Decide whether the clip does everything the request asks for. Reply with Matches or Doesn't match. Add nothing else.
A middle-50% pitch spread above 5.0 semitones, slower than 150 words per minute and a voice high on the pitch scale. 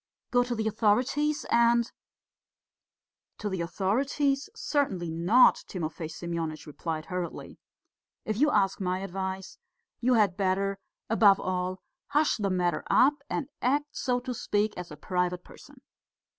Matches